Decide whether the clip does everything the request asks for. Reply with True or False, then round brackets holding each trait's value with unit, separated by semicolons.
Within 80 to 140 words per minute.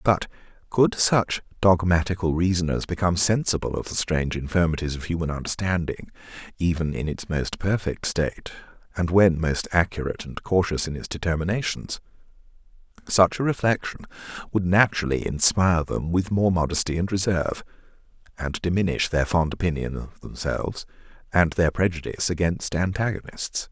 True (135 wpm)